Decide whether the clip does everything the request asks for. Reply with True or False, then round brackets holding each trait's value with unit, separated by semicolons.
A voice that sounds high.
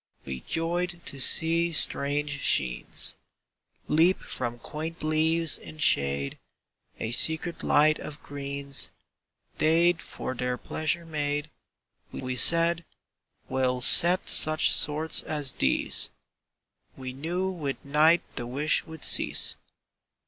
False (150 Hz)